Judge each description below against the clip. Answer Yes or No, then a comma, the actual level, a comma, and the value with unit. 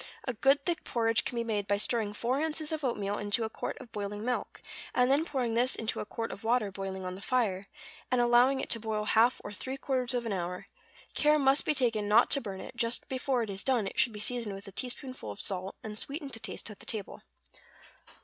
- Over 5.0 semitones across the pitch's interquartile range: No, average, 3.8 semitones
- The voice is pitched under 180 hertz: No, high, 230 Hz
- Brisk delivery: Yes, fast, 240 wpm